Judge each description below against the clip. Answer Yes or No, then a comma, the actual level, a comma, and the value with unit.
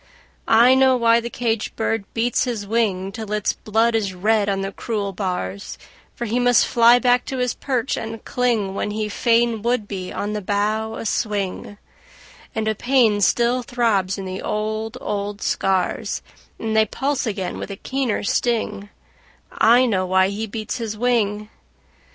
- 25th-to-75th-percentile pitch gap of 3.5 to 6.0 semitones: No, average, 2.8 semitones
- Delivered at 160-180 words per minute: Yes, average, 170 wpm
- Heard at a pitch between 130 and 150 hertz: No, high, 220 Hz